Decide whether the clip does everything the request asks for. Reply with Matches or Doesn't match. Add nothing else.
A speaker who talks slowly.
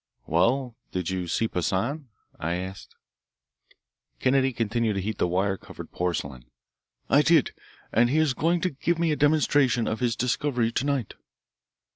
Doesn't match